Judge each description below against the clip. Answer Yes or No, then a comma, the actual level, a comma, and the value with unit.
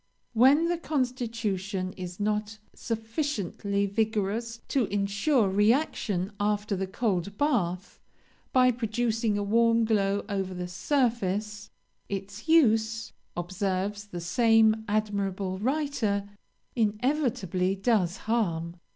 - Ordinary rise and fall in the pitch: Yes, average, 3.0 semitones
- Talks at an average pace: No, slow, 100 wpm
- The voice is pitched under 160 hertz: No, high, 210 Hz